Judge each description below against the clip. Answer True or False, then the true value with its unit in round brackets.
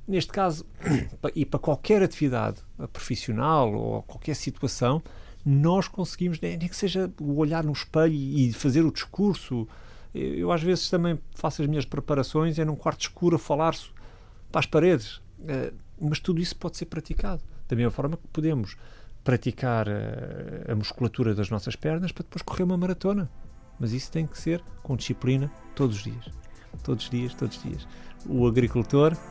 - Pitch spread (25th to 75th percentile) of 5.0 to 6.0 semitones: True (5.3 semitones)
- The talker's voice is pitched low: False (145 Hz)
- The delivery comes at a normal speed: True (165 wpm)